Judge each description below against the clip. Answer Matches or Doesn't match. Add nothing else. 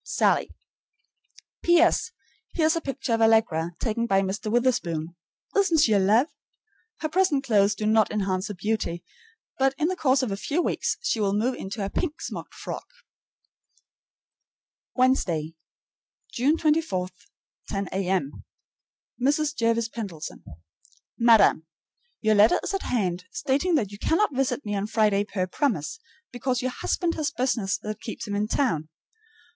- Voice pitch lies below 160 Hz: Doesn't match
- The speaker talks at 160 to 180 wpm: Doesn't match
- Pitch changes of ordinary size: Doesn't match